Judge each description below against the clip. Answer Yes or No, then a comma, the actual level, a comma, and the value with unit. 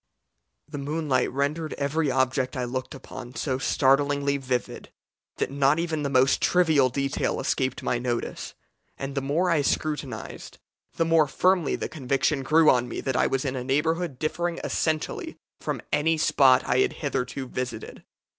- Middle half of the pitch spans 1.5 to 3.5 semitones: Yes, average, 3.0 semitones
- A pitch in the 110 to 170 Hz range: Yes, medium, 140 Hz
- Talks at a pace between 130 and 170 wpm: Yes, average, 160 wpm